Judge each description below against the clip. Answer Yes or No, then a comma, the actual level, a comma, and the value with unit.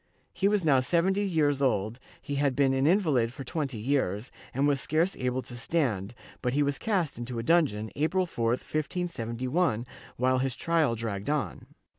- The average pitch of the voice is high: No, low, 135 Hz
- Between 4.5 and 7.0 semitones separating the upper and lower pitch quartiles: Yes, average, 5.1 semitones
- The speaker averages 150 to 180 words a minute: Yes, average, 175 wpm